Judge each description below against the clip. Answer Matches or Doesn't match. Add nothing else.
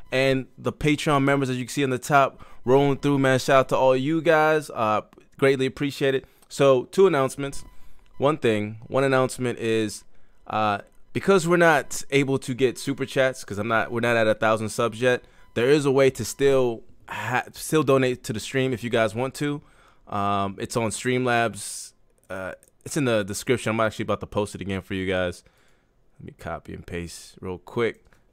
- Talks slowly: Doesn't match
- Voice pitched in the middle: Doesn't match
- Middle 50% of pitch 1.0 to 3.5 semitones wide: Doesn't match